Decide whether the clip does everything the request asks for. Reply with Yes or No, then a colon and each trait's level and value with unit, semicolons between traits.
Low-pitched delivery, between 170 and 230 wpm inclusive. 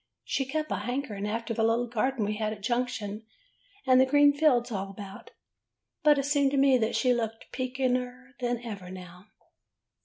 No: high, 245 Hz; average, 180 wpm